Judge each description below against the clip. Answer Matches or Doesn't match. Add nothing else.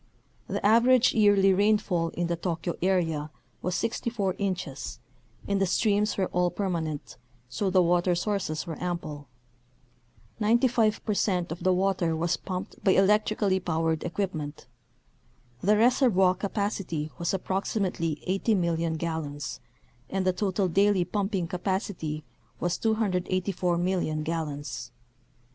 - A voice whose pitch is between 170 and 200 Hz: Matches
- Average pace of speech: Doesn't match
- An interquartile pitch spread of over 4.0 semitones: Doesn't match